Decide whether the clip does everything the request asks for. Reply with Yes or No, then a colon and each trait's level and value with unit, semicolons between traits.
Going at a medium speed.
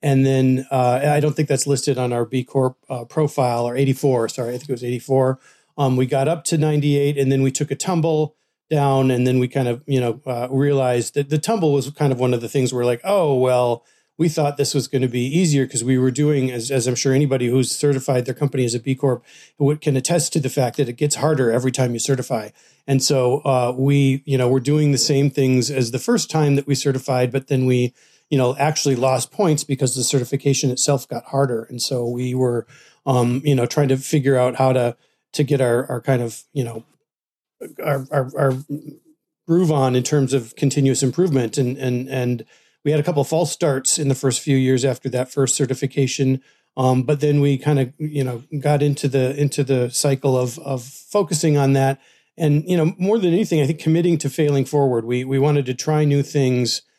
No: fast, 230 wpm